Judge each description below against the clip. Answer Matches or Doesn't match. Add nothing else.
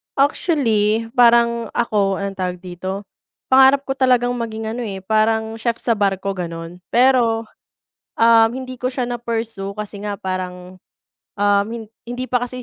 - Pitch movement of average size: Matches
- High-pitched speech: Matches